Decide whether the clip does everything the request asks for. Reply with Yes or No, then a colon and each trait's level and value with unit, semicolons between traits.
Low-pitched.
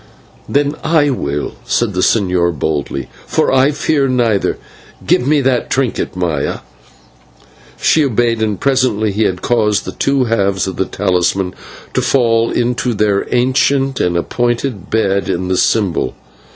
Yes: low, 110 Hz